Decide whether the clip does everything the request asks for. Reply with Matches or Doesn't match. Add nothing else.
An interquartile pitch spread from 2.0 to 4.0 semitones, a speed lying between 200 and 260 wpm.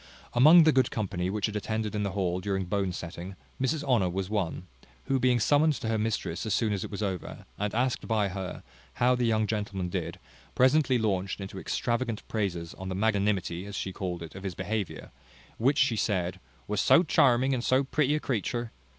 Doesn't match